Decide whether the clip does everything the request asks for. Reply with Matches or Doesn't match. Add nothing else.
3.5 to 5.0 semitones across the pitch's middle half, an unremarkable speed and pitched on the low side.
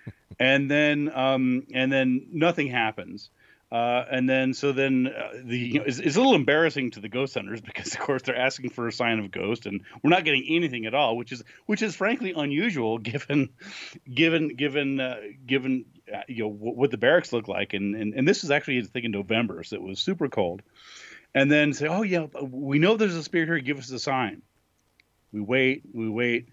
Doesn't match